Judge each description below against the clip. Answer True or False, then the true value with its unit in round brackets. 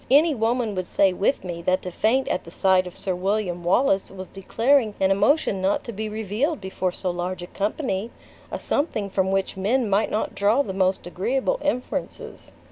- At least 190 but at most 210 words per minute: True (195 wpm)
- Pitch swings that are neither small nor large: True (4.0 semitones)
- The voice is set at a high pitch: True (200 Hz)